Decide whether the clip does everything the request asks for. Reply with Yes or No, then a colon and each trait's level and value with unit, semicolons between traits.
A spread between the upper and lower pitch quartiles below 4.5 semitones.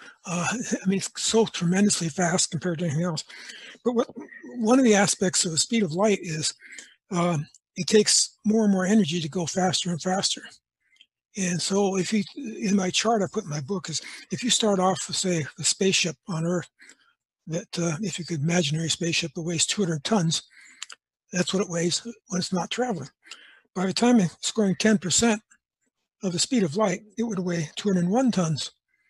Yes: average, 3.9 semitones